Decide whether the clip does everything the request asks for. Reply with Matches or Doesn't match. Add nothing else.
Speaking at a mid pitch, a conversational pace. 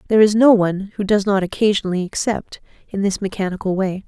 Doesn't match